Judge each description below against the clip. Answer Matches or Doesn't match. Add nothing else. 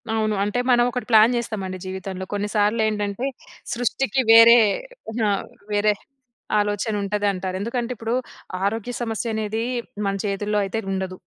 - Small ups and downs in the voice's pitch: Matches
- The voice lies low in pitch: Doesn't match